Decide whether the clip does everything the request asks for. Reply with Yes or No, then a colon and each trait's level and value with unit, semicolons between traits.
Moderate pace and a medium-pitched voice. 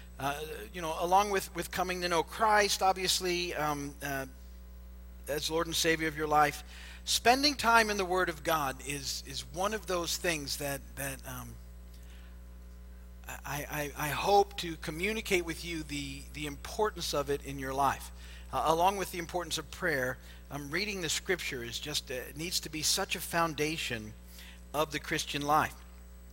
Yes: average, 170 wpm; medium, 150 Hz